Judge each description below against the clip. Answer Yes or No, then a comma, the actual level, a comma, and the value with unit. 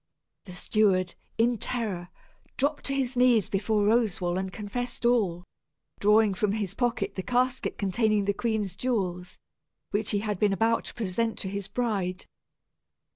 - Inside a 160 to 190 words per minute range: No, average, 150 wpm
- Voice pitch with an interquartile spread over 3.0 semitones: Yes, average, 3.5 semitones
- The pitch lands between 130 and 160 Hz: No, high, 210 Hz